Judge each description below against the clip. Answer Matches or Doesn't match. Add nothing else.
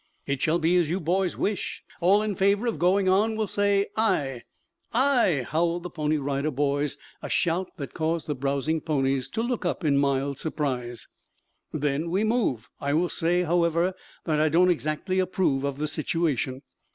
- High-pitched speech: Doesn't match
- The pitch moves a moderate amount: Matches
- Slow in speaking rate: Doesn't match